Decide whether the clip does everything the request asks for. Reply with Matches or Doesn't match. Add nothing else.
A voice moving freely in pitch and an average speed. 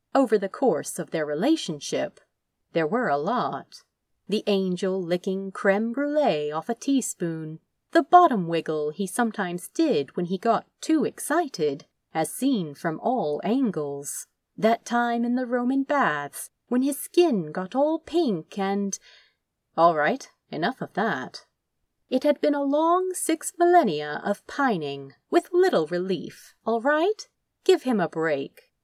Matches